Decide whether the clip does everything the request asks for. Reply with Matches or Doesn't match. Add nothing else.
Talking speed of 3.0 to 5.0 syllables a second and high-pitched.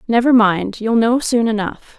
Matches